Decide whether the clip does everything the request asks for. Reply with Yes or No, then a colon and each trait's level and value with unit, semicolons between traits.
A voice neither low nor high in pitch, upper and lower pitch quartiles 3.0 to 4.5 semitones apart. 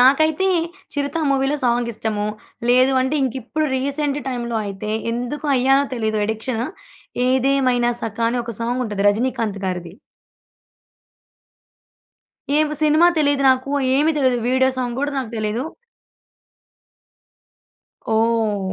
No: very high, 250 Hz; average, 3.6 semitones